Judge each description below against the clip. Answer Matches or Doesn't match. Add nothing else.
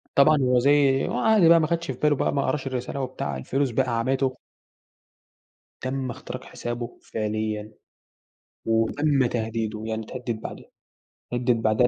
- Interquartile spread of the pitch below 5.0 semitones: Matches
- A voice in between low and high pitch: Doesn't match